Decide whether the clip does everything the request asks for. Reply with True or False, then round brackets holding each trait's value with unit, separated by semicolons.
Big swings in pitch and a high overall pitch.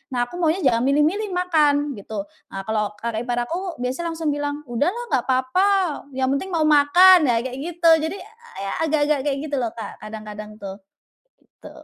True (5.8 semitones; 285 Hz)